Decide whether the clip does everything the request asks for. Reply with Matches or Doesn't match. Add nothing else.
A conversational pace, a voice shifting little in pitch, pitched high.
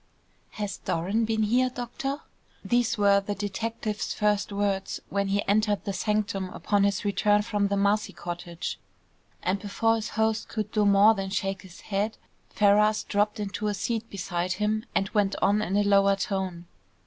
Matches